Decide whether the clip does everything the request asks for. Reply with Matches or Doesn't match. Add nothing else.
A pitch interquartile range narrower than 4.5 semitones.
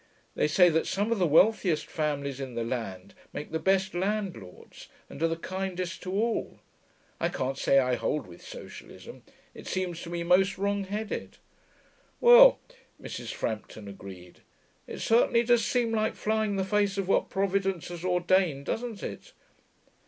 Doesn't match